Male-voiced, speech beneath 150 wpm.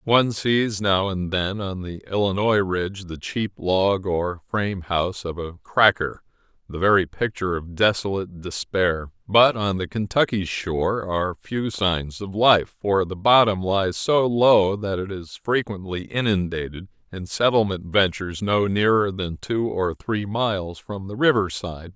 No: male; average, 160 wpm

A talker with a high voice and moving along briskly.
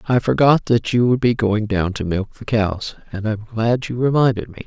No: low, 115 Hz; fast, 230 wpm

